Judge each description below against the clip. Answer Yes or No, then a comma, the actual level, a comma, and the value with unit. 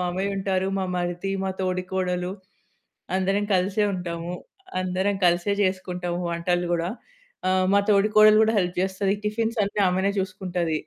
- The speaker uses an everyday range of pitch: No, narrow, 1.7 semitones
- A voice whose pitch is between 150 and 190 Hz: Yes, medium, 185 Hz